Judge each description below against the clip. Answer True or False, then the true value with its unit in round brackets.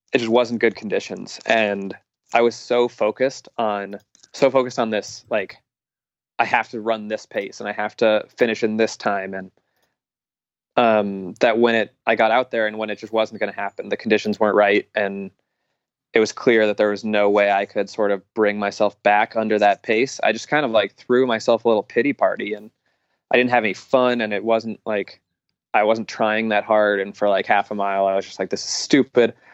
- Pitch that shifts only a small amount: True (1.9 semitones)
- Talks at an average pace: False (220 wpm)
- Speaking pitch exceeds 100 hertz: True (110 Hz)